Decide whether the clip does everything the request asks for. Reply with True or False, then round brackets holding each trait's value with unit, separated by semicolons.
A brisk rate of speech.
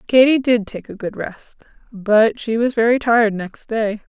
False (190 wpm)